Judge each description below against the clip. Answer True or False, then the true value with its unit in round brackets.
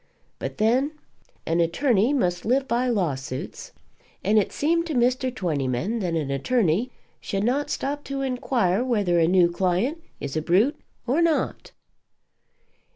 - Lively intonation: True (7.1 semitones)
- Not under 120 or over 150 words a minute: True (145 wpm)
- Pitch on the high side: True (220 Hz)